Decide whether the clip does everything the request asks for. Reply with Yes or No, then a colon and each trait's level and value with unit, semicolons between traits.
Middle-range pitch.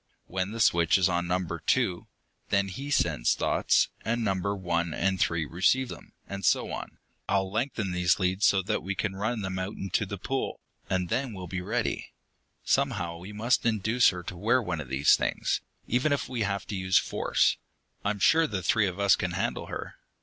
No: very low, 95 Hz